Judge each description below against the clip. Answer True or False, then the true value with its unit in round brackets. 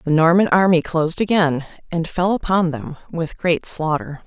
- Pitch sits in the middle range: True (165 Hz)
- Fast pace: False (170 wpm)